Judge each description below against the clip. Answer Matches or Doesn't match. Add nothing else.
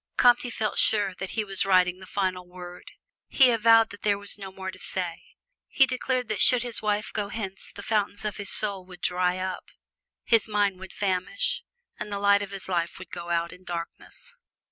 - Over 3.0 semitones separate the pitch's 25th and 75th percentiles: Doesn't match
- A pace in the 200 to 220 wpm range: Matches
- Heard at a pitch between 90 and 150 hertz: Doesn't match